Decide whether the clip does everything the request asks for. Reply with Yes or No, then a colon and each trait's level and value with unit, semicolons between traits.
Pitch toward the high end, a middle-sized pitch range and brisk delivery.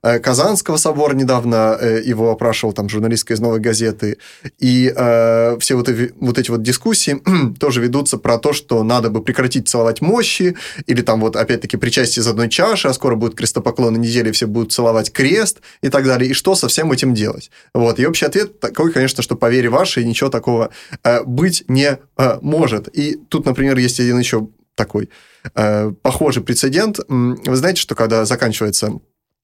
No: low, 125 Hz; average, 3.0 semitones; fast, 180 wpm